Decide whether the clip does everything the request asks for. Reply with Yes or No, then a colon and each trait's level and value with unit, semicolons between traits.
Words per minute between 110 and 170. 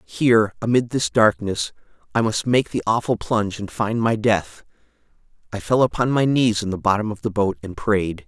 No: average, 195 wpm